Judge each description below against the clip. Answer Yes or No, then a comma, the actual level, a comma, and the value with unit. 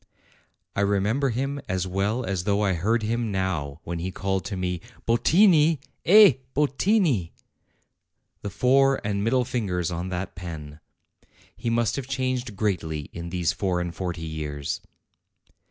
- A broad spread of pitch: Yes, wide, 6.1 semitones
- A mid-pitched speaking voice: No, low, 100 Hz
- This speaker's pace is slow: No, average, 145 wpm